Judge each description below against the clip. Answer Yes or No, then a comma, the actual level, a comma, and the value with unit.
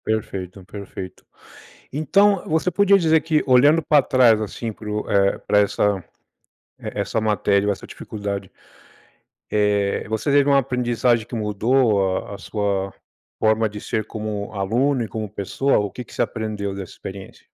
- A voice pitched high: No, low, 110 Hz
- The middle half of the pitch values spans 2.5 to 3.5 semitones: No, average, 4.2 semitones